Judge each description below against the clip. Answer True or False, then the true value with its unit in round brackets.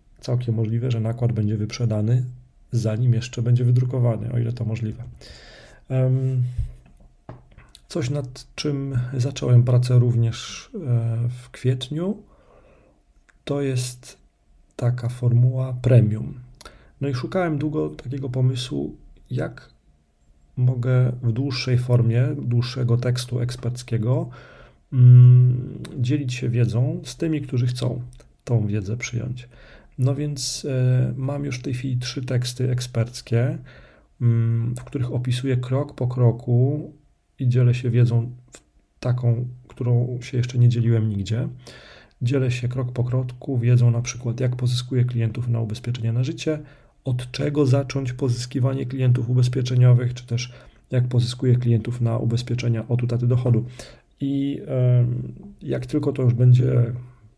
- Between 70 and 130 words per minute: True (125 wpm)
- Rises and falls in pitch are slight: True (1.4 semitones)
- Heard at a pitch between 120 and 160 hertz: True (125 Hz)